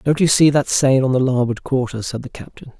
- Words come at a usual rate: No, fast, 260 wpm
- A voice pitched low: Yes, low, 130 Hz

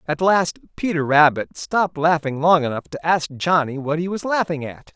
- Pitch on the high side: No, medium, 155 Hz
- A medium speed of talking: Yes, average, 195 wpm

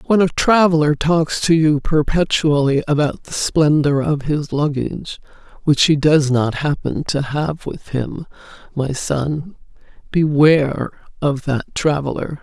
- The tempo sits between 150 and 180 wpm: No, slow, 135 wpm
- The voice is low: No, medium, 150 Hz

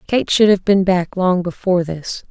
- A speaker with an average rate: No, fast, 210 wpm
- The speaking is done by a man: No, female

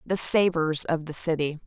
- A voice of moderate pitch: Yes, medium, 165 Hz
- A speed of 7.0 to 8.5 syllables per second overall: No, 4.7 syllables/s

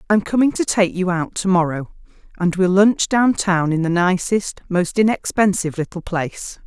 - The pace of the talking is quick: No, average, 180 wpm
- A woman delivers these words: Yes, female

